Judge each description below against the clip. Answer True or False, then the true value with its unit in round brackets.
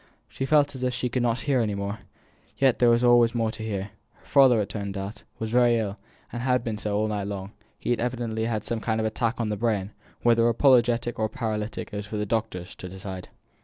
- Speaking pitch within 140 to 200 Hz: False (110 Hz)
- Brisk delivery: True (240 wpm)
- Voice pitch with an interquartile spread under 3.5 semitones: True (2.5 semitones)